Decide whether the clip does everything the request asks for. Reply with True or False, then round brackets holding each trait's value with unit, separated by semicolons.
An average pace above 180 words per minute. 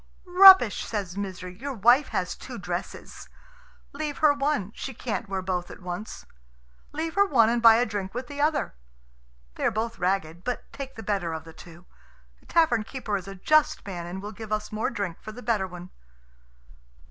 True (195 wpm)